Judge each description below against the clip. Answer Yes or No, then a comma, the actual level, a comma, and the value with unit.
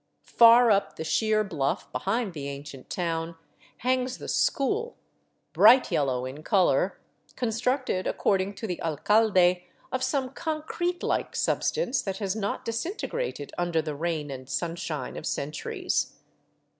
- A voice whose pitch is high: Yes, high, 195 Hz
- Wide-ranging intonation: Yes, wide, 7.8 semitones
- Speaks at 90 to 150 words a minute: Yes, slow, 135 wpm